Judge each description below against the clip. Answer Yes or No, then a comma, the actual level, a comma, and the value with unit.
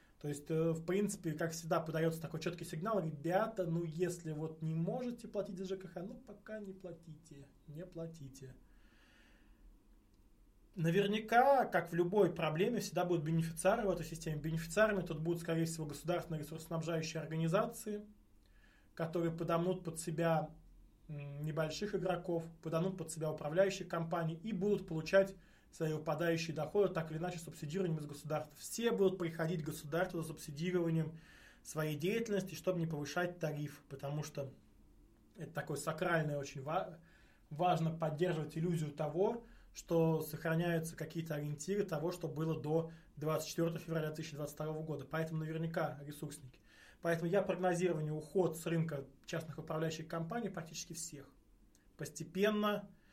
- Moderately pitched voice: Yes, medium, 165 Hz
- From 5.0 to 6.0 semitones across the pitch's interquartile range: No, narrow, 2.6 semitones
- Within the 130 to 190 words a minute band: Yes, average, 135 wpm